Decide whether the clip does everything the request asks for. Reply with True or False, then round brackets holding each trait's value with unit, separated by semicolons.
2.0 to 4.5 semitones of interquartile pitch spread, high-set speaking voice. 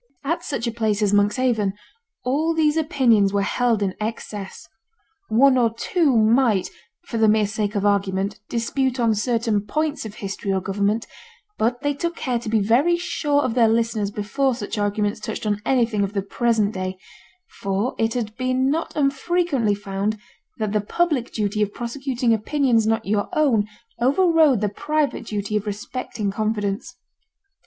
True (4.2 semitones; 225 Hz)